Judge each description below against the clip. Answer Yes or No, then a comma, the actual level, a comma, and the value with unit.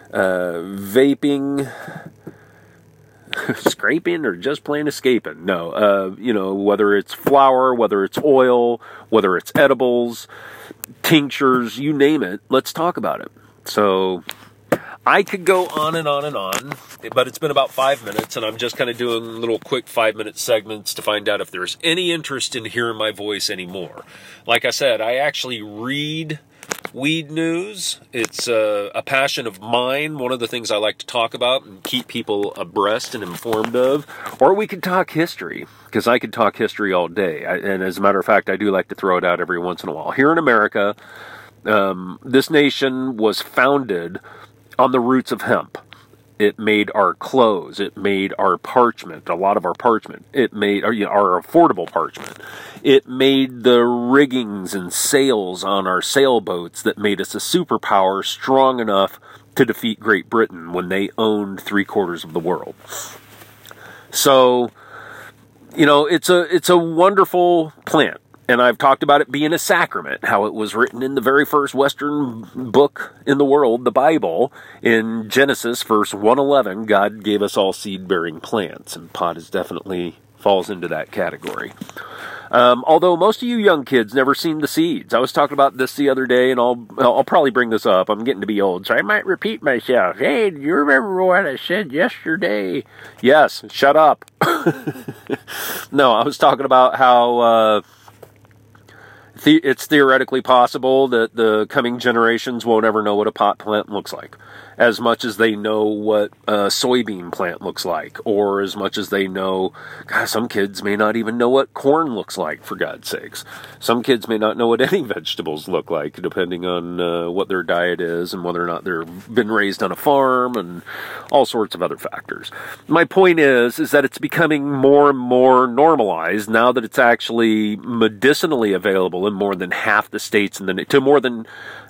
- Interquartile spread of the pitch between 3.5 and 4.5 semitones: No, average, 5.2 semitones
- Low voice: Yes, low, 120 Hz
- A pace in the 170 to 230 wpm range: Yes, average, 180 wpm